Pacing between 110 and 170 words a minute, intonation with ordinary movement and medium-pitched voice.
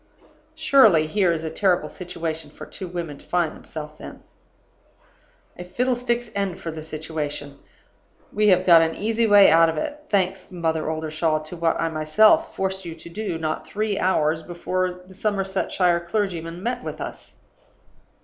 Yes: average, 160 wpm; average, 3.9 semitones; medium, 175 Hz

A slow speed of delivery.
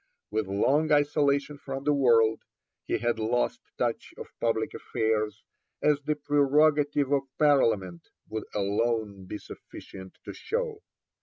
Yes: slow, 130 wpm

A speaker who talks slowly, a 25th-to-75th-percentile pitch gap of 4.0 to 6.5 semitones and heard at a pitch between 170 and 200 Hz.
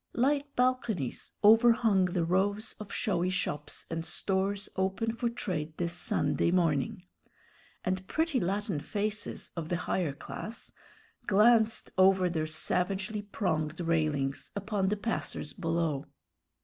Yes: slow, 125 wpm; average, 4.3 semitones; high, 190 Hz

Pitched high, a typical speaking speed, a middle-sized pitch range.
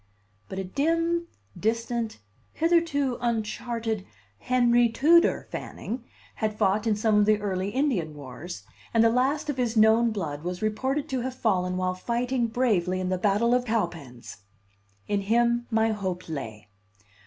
Yes: high, 220 Hz; average, 150 wpm; average, 4.7 semitones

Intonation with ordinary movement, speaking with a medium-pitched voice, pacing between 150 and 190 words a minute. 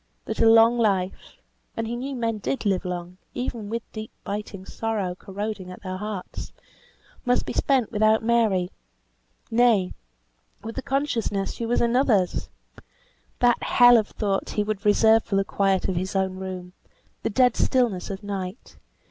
No: average, 3.4 semitones; high, 215 Hz; average, 160 wpm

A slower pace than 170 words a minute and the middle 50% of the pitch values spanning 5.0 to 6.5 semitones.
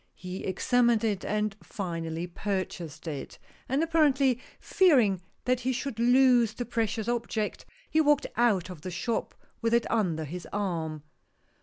Yes: average, 145 wpm; average, 5.3 semitones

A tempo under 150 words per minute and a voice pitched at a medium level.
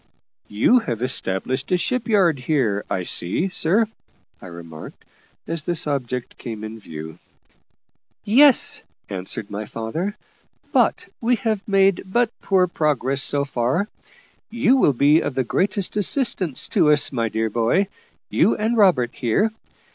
Yes: average, 140 wpm; medium, 145 Hz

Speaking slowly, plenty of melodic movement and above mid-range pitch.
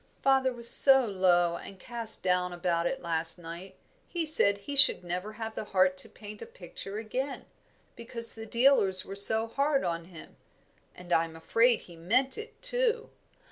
No: average, 180 wpm; wide, 6.4 semitones; high, 210 Hz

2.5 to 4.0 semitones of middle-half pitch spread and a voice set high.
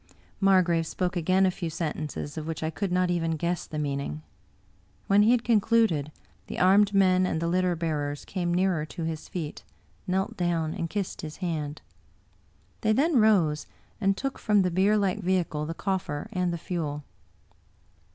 No: average, 3.4 semitones; medium, 175 Hz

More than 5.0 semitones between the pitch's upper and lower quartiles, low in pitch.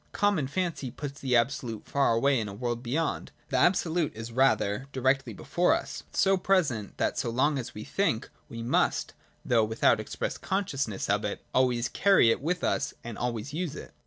Yes: wide, 5.4 semitones; low, 130 Hz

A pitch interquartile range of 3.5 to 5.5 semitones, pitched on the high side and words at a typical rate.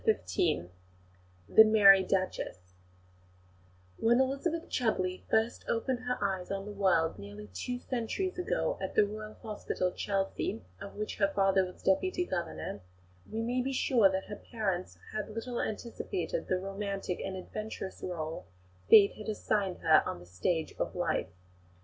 Yes: average, 3.8 semitones; high, 200 Hz; average, 150 wpm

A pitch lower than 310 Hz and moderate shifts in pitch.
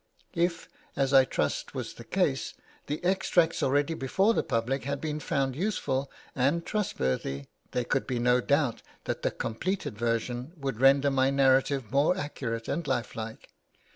Yes: low, 135 Hz; average, 3.4 semitones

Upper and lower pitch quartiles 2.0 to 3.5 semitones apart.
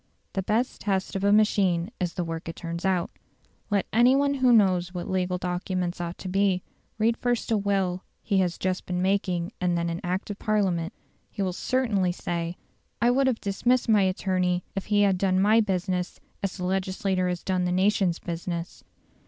Yes: narrow, 2.4 semitones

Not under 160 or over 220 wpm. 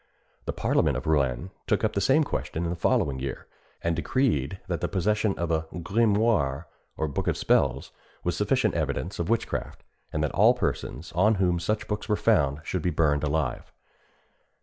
Yes: average, 180 wpm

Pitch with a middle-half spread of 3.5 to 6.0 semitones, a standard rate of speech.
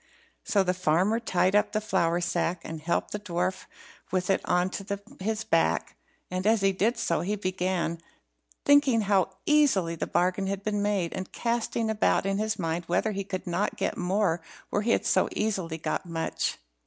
No: average, 3.0 semitones; average, 185 wpm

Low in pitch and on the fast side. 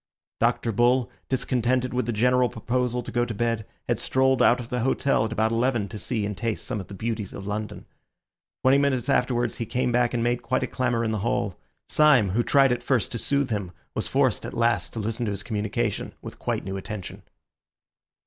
Yes: low, 120 Hz; fast, 215 wpm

